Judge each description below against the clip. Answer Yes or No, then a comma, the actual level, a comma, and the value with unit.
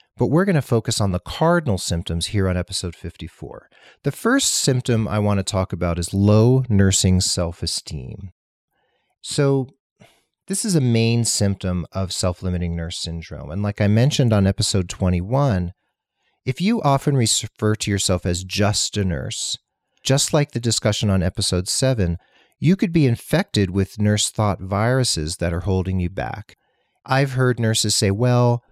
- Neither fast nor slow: Yes, average, 165 wpm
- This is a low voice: Yes, low, 105 Hz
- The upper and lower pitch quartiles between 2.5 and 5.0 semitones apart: No, wide, 5.6 semitones